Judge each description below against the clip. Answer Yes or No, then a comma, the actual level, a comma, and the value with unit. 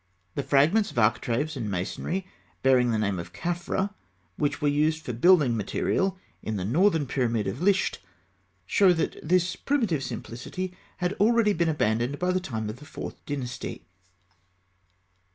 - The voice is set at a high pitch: No, medium, 150 Hz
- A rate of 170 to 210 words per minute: No, average, 150 wpm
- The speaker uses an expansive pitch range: Yes, wide, 7.5 semitones